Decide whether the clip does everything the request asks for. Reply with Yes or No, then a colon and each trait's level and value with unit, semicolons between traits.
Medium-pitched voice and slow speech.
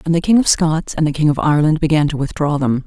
No: medium, 155 Hz; fast, 295 wpm